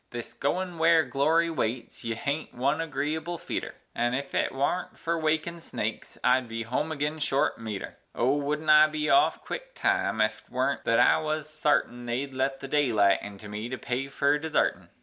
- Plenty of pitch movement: No, average, 4.3 semitones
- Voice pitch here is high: No, medium, 140 Hz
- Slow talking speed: No, average, 185 wpm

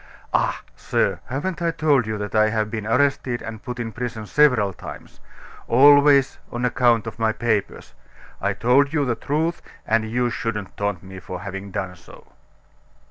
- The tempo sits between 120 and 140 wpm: No, average, 170 wpm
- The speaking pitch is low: Yes, low, 115 Hz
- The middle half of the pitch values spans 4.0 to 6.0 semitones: Yes, average, 4.4 semitones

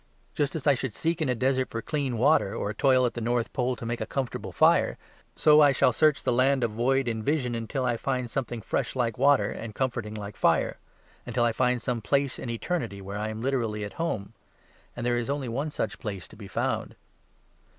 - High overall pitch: No, low, 125 Hz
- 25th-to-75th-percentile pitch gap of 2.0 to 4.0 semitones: Yes, average, 3.1 semitones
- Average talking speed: No, fast, 225 wpm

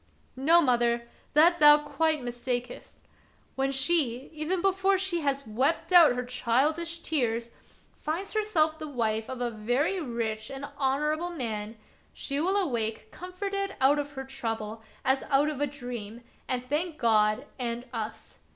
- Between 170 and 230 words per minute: No, average, 150 wpm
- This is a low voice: No, very high, 270 Hz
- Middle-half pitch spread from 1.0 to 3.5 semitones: No, average, 5.2 semitones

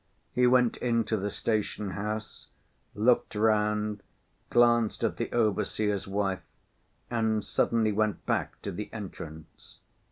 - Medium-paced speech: No, slow, 120 wpm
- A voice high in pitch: No, low, 105 Hz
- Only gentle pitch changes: Yes, narrow, 1.9 semitones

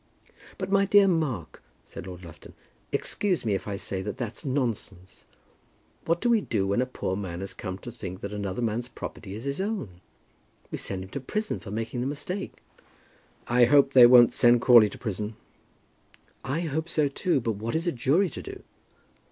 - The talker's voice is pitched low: Yes, low, 120 Hz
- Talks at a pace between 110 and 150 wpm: No, average, 195 wpm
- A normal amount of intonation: No, wide, 7.2 semitones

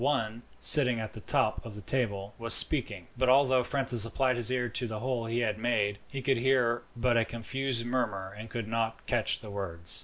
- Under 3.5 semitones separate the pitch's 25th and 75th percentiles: Yes, average, 2.8 semitones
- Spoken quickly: Yes, fast, 210 wpm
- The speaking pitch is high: No, low, 115 Hz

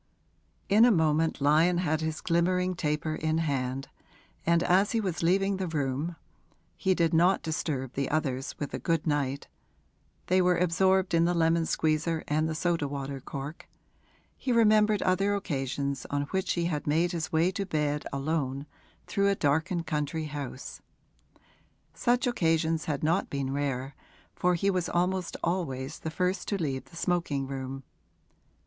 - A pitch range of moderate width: Yes, average, 4.0 semitones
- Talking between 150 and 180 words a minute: Yes, average, 160 wpm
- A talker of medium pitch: Yes, medium, 160 Hz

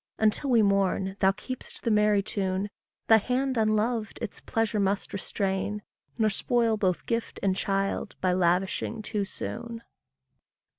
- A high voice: Yes, high, 210 Hz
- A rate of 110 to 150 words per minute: Yes, average, 140 wpm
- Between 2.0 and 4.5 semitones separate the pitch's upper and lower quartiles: Yes, narrow, 2.6 semitones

